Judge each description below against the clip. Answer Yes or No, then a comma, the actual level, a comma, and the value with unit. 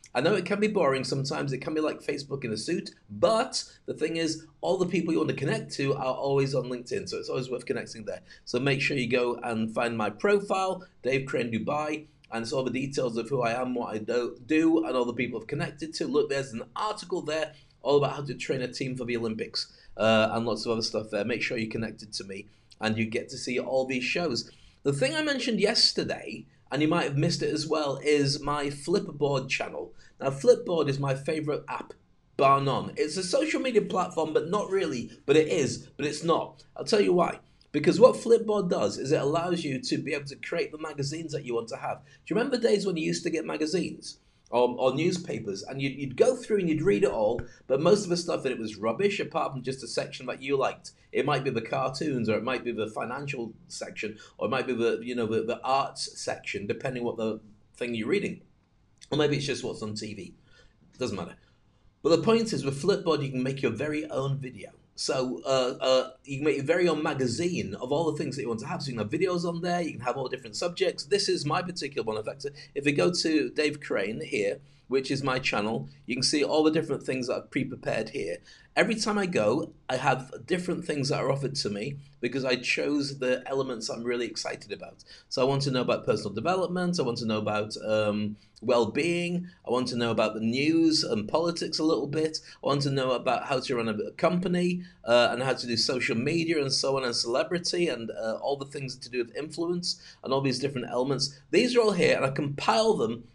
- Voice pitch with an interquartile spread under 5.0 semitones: No, average, 5.3 semitones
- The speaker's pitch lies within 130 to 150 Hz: Yes, medium, 140 Hz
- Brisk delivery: Yes, fast, 240 wpm